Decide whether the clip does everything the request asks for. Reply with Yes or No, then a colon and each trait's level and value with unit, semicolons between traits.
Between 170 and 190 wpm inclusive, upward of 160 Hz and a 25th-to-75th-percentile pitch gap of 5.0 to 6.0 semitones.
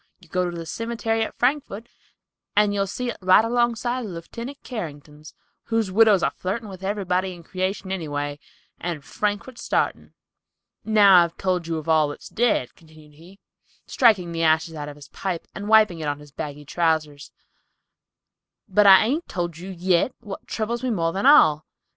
Yes: average, 180 wpm; medium, 185 Hz; average, 5.3 semitones